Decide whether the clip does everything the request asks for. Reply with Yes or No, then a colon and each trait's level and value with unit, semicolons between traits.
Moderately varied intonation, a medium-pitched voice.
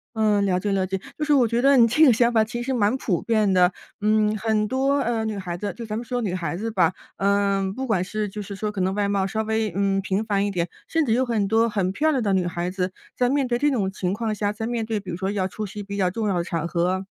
No: average, 3.1 semitones; high, 210 Hz